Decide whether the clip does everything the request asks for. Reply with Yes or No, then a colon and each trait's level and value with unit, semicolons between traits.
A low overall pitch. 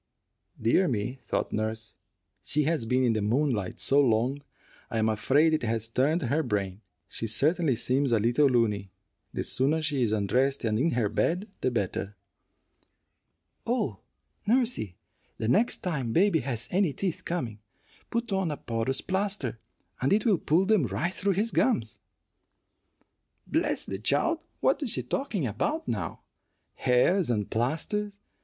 Yes: low, 130 Hz